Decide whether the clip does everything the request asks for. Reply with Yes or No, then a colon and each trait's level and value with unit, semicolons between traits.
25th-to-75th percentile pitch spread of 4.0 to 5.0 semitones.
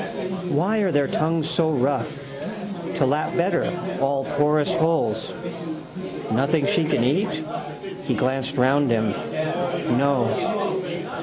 Yes: average, 4.5 semitones